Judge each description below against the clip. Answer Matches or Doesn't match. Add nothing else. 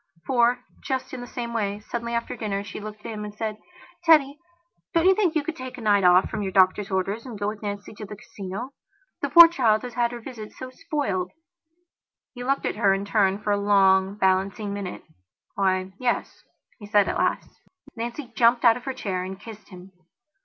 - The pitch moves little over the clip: Doesn't match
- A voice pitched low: Doesn't match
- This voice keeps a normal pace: Doesn't match